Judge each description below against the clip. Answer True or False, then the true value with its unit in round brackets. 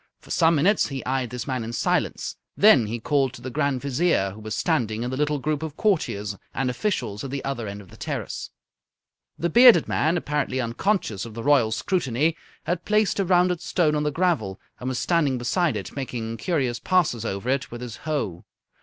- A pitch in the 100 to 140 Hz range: True (135 Hz)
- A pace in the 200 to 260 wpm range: True (205 wpm)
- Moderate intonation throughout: False (5.9 semitones)